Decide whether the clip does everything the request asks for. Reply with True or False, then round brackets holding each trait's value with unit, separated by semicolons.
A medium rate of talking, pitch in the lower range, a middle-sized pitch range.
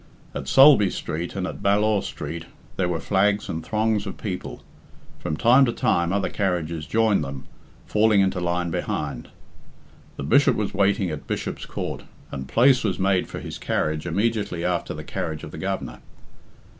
True (170 wpm; 95 Hz; 3.9 semitones)